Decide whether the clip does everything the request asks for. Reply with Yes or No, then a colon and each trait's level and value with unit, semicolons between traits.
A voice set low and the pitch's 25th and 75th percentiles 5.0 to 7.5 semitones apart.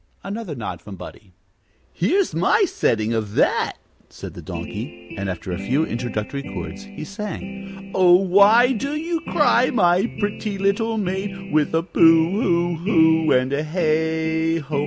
No: medium, 175 Hz; average, 5.3 semitones